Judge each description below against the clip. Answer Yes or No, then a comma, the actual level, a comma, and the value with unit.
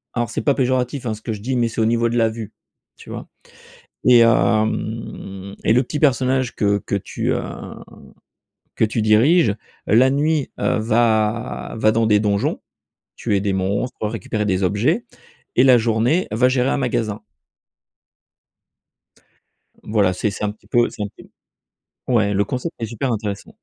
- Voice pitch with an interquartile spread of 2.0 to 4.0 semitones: Yes, average, 3.0 semitones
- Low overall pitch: Yes, low, 115 Hz